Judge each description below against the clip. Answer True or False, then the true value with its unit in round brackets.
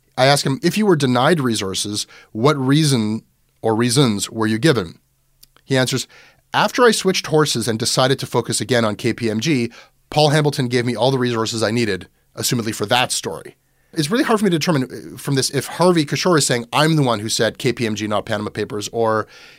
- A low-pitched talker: True (125 Hz)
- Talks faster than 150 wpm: True (200 wpm)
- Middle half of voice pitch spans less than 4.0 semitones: False (4.7 semitones)